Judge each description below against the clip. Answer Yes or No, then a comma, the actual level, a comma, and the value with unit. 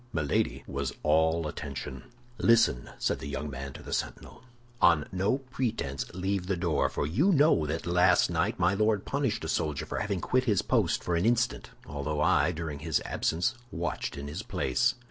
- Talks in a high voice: No, very low, 85 Hz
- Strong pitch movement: Yes, wide, 6.4 semitones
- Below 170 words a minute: No, average, 185 wpm